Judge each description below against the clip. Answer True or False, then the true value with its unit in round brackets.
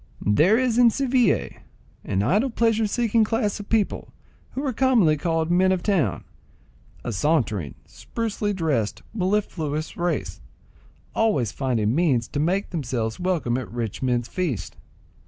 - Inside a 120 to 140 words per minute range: True (135 wpm)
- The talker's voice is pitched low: False (175 Hz)